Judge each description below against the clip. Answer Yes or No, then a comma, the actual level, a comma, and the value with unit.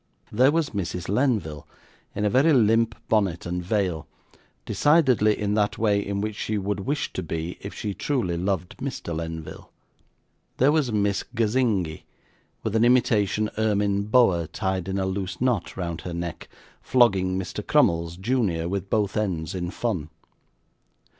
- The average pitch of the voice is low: Yes, low, 100 Hz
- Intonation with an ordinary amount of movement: Yes, average, 4.0 semitones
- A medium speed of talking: Yes, average, 155 wpm